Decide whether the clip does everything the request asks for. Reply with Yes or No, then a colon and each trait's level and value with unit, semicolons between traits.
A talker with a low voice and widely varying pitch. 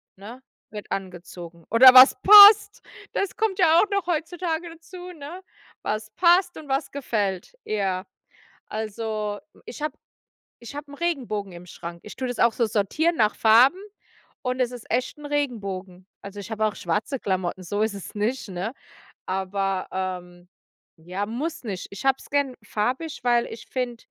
No: high, 230 Hz; wide, 6.8 semitones